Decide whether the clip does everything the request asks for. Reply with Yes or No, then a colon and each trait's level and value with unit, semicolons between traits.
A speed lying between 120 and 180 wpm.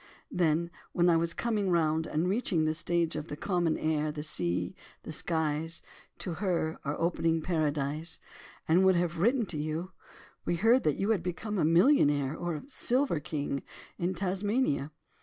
Yes: average, 170 wpm